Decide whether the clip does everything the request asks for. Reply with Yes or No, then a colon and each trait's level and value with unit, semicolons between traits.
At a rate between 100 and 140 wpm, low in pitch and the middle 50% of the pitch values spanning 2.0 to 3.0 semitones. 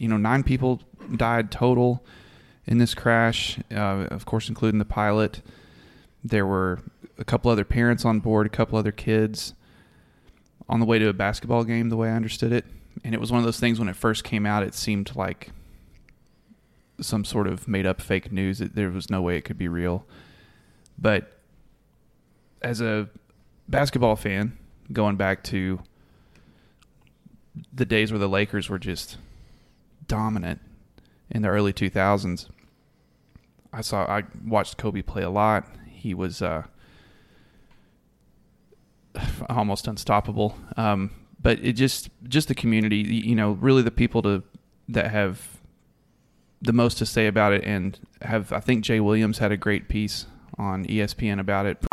No: average, 160 wpm; low, 110 Hz; average, 2.7 semitones